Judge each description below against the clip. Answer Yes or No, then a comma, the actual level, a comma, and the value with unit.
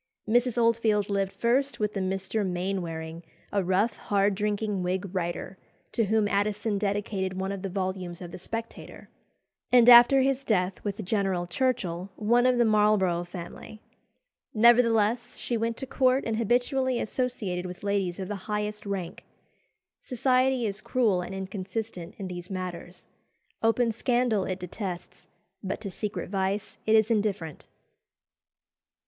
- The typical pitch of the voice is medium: No, high, 205 Hz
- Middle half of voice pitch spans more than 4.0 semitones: No, average, 3.5 semitones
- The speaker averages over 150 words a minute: No, average, 145 wpm